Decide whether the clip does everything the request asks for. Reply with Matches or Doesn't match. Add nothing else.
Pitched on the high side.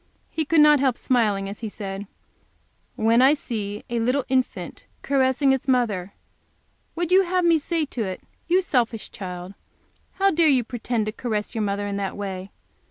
Matches